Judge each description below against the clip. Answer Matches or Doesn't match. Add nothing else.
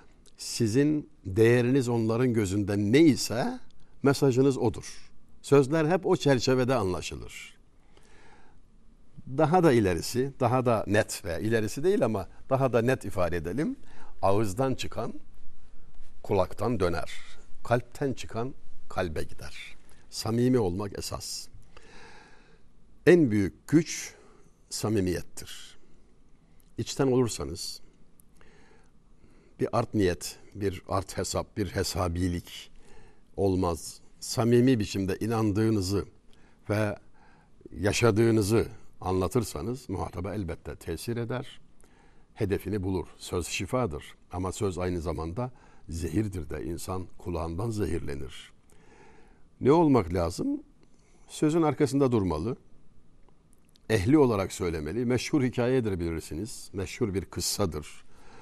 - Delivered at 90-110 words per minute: Matches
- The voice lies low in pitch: Matches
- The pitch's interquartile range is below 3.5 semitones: Doesn't match